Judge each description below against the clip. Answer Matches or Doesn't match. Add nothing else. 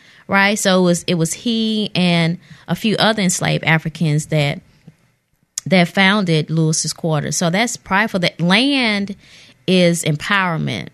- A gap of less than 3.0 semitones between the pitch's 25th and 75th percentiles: Doesn't match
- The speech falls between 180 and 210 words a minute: Doesn't match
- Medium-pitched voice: Matches